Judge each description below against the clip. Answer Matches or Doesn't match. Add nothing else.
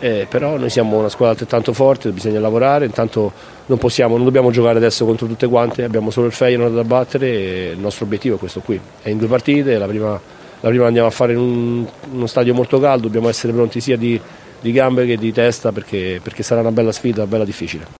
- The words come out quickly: Matches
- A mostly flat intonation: Matches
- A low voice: Matches